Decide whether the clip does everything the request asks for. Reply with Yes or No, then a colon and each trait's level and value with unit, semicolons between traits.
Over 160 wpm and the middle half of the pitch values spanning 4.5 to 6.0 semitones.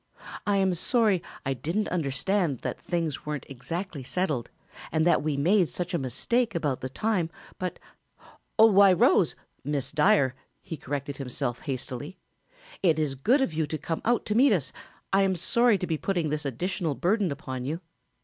Yes: average, 170 wpm; wide, 5.5 semitones